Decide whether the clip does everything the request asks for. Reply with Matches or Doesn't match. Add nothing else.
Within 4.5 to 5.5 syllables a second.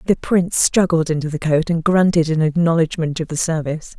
Doesn't match